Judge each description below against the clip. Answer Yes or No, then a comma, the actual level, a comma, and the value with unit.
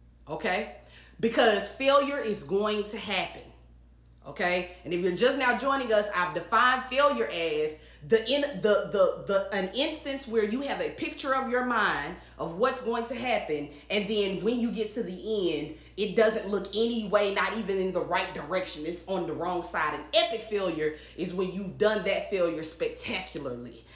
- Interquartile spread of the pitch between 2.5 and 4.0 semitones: No, average, 5.0 semitones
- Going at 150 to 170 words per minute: No, average, 185 wpm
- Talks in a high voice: Yes, high, 210 Hz